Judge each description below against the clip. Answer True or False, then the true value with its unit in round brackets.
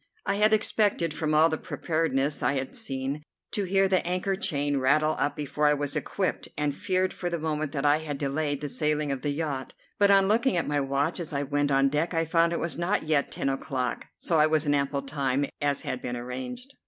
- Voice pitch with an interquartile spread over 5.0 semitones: False (3.3 semitones)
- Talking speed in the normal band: False (230 wpm)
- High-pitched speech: False (150 Hz)